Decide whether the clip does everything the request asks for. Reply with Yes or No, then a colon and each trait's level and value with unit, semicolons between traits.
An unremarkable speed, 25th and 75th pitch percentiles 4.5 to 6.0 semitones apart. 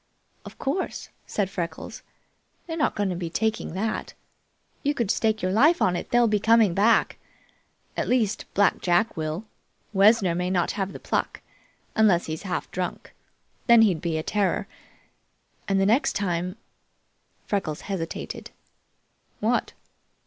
No: average, 150 wpm; average, 3.9 semitones